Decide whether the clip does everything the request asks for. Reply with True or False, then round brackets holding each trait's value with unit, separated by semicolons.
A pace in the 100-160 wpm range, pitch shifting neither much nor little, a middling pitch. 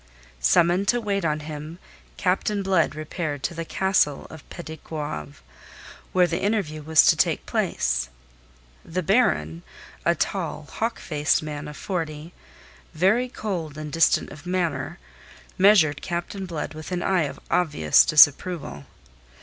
True (140 wpm; 3.7 semitones; 160 Hz)